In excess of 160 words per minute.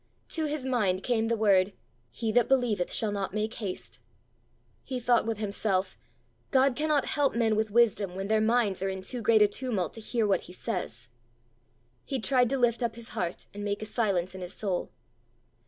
Yes: average, 195 wpm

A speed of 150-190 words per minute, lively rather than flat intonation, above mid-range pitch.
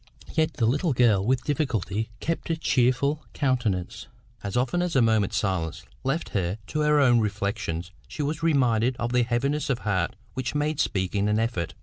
No: average, 180 wpm; wide, 6.0 semitones; low, 120 Hz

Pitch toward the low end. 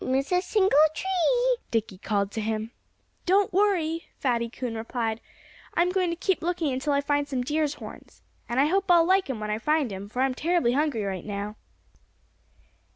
No: very high, 285 Hz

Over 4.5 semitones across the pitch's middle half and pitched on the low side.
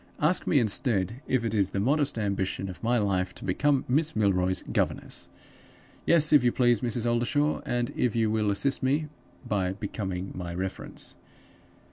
Yes: average, 5.2 semitones; low, 115 Hz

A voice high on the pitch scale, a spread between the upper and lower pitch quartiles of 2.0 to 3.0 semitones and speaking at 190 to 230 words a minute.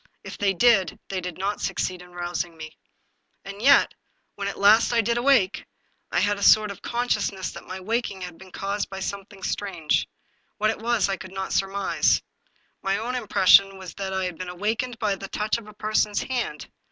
Yes: high, 200 Hz; narrow, 2.5 semitones; fast, 205 wpm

